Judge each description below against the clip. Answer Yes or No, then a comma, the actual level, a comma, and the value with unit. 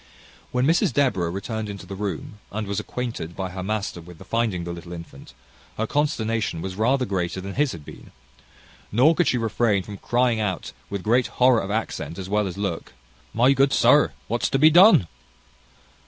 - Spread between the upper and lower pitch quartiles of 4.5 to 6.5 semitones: Yes, average, 4.8 semitones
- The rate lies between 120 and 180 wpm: No, average, 190 wpm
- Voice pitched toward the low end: Yes, low, 105 Hz